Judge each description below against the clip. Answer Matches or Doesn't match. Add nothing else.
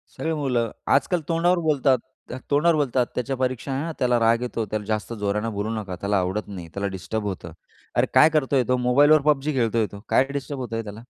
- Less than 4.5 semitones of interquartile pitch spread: Doesn't match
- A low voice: Matches